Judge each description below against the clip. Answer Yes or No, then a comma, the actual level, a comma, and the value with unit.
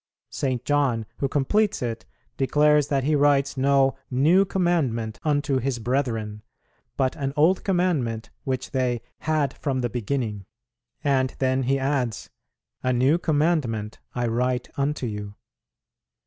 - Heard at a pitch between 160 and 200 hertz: No, low, 135 Hz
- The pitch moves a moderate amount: Yes, average, 3.2 semitones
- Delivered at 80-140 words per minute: Yes, slow, 135 wpm